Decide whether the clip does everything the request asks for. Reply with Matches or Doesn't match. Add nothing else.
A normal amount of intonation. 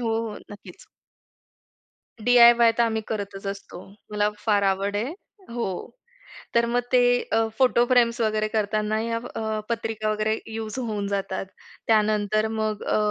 Doesn't match